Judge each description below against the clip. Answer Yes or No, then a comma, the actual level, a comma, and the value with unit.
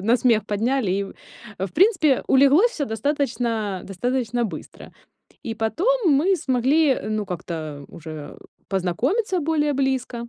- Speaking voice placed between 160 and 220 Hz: No, high, 245 Hz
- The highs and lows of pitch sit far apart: Yes, wide, 5.8 semitones